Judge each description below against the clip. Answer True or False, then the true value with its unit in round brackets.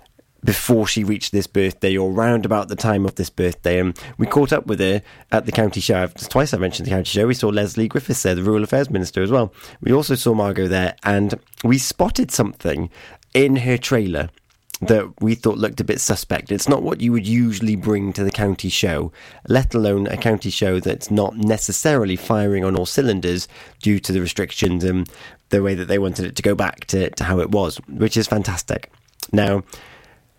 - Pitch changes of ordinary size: True (3.3 semitones)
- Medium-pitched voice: False (105 Hz)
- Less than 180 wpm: False (205 wpm)